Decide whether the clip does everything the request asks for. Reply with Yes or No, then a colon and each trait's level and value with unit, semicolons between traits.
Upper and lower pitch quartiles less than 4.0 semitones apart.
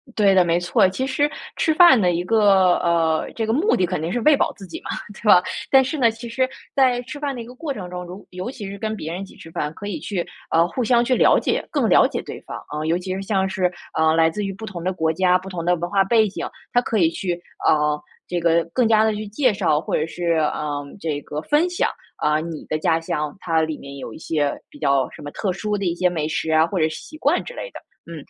No: average, 5.3 semitones